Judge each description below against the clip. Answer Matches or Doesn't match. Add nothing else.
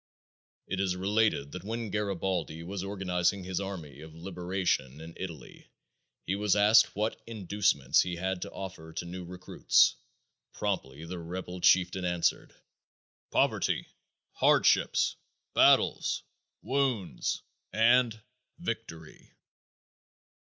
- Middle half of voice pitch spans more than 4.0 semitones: Doesn't match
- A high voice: Doesn't match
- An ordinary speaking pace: Doesn't match